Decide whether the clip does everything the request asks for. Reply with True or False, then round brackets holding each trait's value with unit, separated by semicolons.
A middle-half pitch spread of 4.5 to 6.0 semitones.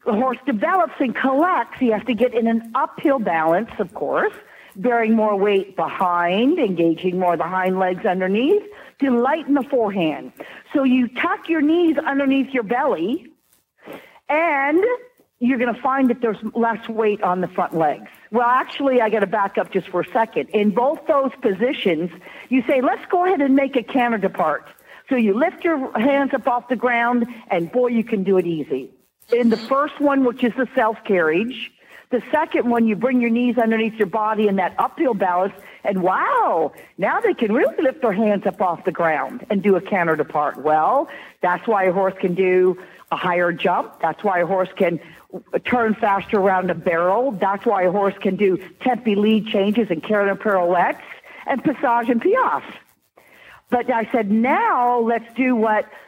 True (5.5 semitones)